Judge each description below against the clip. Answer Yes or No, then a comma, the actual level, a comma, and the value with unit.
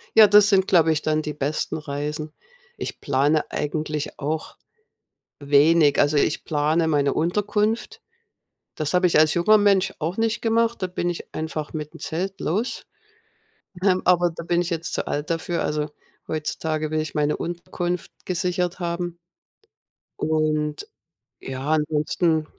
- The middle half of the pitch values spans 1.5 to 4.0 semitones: Yes, average, 2.9 semitones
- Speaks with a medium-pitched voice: Yes, medium, 160 Hz